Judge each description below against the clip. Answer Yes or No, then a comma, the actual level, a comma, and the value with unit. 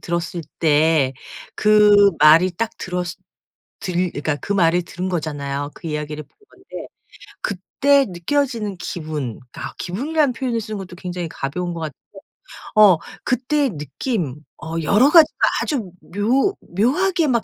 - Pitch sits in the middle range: Yes, medium, 180 Hz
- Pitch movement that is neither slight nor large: No, wide, 6.4 semitones